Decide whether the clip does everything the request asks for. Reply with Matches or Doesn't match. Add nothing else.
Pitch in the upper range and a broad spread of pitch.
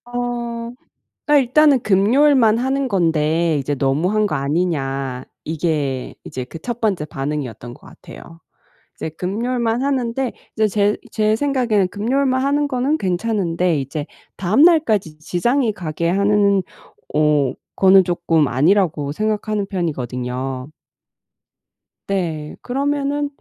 Matches